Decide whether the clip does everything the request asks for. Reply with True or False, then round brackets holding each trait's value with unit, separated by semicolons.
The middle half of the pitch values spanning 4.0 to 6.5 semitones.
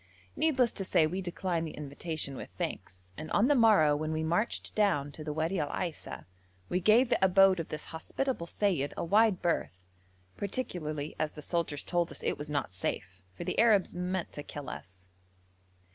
True (4.6 semitones)